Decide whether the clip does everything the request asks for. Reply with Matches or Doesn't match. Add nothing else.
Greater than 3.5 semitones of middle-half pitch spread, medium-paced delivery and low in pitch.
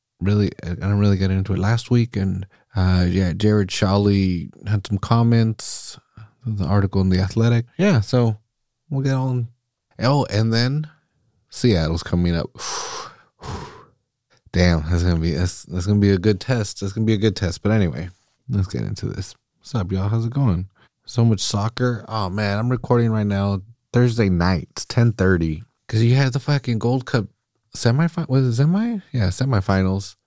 Matches